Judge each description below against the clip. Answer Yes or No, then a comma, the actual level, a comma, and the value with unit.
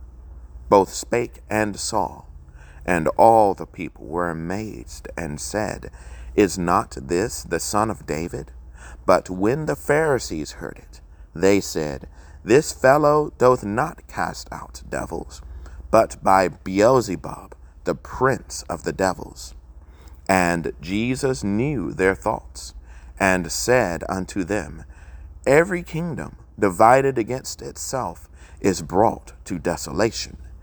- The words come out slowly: Yes, slow, 120 wpm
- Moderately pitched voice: No, very low, 80 Hz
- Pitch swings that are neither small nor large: No, wide, 6.0 semitones